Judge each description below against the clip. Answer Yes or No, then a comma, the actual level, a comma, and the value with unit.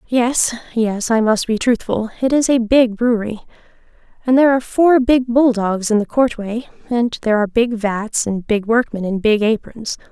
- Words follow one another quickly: No, average, 180 wpm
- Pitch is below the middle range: No, high, 230 Hz